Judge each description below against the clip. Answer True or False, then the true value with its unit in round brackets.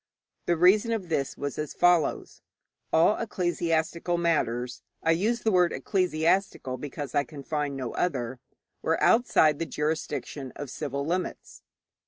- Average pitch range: True (3.9 semitones)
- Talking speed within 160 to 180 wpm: False (140 wpm)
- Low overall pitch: False (160 Hz)